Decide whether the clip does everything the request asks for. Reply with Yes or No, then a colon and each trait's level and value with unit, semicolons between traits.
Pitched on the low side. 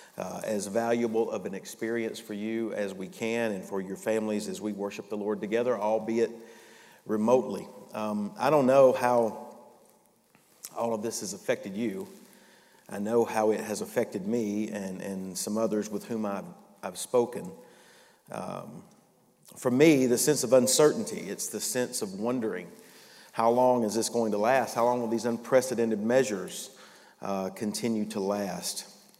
Yes: low, 115 Hz